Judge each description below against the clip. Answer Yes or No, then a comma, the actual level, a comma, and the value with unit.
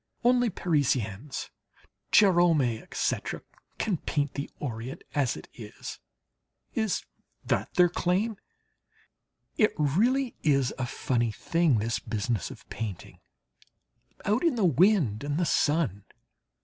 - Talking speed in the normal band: No, slow, 115 wpm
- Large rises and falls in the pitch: Yes, wide, 7.9 semitones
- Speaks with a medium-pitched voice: Yes, medium, 150 Hz